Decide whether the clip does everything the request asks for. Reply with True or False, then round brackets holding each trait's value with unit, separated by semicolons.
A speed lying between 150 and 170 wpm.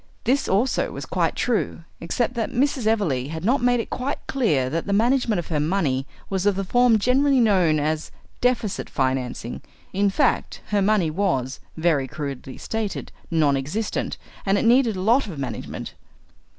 True (165 wpm)